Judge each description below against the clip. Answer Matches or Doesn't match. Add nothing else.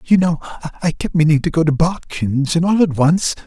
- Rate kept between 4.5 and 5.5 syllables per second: Matches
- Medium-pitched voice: Matches